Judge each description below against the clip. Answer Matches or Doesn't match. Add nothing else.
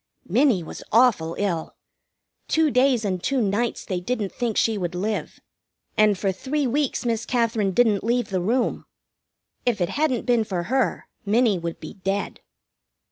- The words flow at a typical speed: Matches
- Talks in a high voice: Matches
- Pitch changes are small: Doesn't match